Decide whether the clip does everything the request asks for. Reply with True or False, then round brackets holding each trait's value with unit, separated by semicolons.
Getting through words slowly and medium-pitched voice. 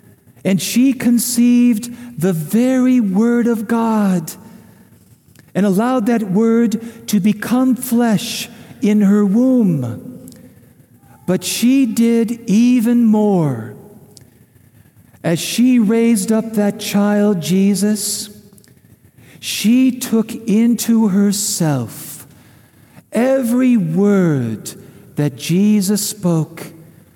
False (85 wpm; 210 Hz)